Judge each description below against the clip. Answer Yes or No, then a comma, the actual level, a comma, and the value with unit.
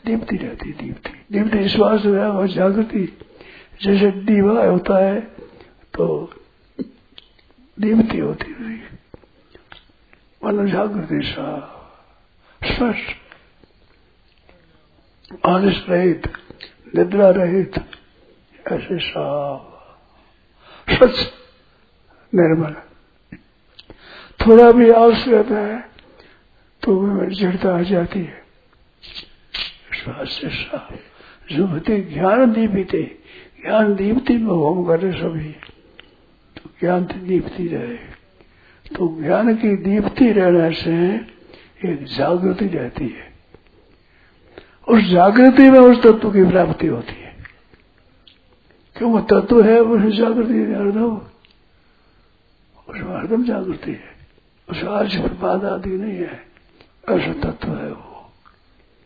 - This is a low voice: No, high, 200 Hz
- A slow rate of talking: Yes, slow, 95 wpm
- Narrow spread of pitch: No, average, 4.5 semitones